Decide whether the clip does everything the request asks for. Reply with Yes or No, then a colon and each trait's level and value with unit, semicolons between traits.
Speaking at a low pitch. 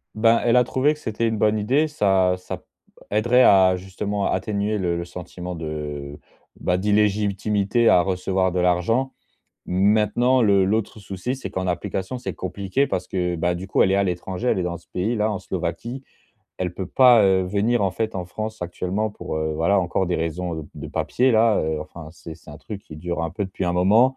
Yes: very low, 95 Hz